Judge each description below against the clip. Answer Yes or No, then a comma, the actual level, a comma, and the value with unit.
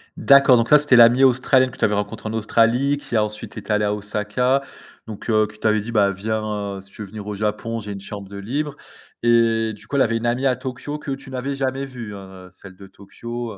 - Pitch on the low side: Yes, low, 115 Hz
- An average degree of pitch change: Yes, average, 3.6 semitones